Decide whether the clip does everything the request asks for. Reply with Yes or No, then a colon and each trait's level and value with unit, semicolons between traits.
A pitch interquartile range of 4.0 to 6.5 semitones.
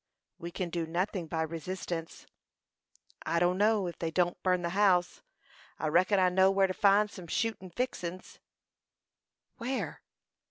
No: narrow, 2.4 semitones